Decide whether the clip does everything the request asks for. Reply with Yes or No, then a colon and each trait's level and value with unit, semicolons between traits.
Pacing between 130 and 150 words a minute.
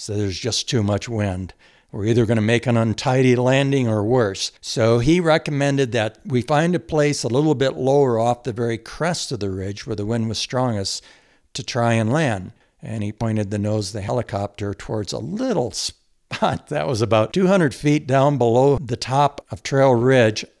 No: average, 200 wpm